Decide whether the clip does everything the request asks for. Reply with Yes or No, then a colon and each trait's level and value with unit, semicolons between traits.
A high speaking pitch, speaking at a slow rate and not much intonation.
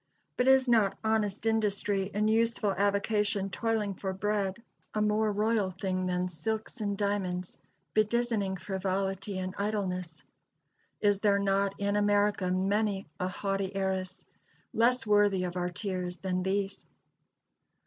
Yes: high, 200 Hz; slow, 130 wpm; narrow, 2.0 semitones